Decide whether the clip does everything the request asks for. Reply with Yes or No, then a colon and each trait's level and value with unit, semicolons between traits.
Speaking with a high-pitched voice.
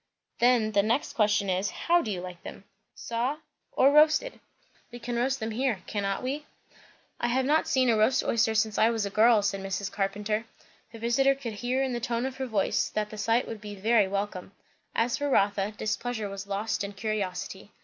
Yes: high, 220 Hz